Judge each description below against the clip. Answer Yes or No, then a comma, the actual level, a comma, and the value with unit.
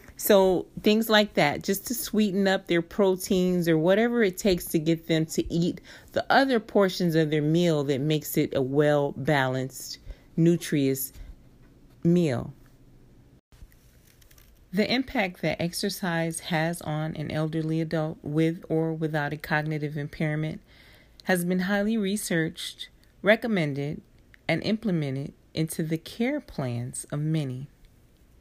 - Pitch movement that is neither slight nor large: Yes, average, 4.2 semitones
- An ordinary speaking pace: No, slow, 130 wpm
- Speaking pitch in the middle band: Yes, medium, 165 Hz